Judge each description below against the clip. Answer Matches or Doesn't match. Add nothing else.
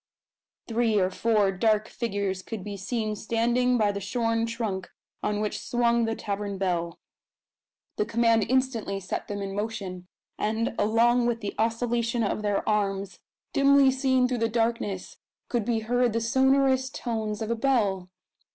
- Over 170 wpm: Doesn't match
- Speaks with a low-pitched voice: Doesn't match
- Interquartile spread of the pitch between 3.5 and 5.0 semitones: Doesn't match